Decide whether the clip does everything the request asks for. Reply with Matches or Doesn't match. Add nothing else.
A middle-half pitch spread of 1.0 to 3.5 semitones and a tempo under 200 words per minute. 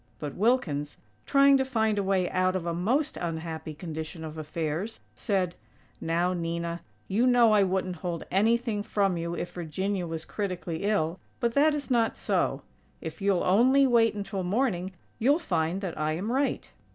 Doesn't match